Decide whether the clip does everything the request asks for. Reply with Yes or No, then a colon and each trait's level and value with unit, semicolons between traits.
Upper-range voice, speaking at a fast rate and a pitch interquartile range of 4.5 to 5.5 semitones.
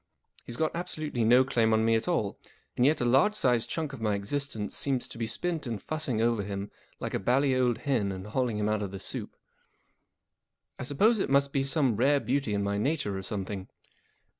No: low, 120 Hz; fast, 215 wpm; average, 4.9 semitones